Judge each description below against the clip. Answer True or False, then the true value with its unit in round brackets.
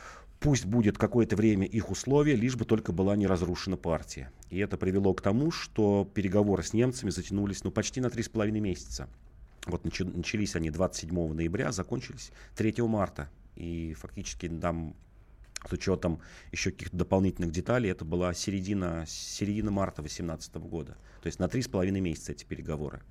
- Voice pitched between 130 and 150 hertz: False (95 Hz)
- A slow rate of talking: False (155 wpm)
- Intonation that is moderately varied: True (4.0 semitones)